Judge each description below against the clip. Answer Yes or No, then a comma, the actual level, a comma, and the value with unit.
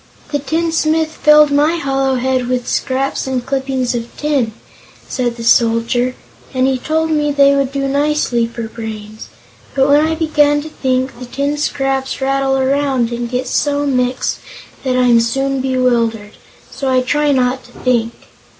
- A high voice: Yes, very high, 265 Hz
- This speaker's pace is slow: No, average, 160 wpm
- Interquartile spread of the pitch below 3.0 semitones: Yes, narrow, 2.5 semitones